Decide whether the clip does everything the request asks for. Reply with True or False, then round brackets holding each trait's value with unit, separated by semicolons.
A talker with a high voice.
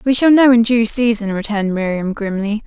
True (220 Hz)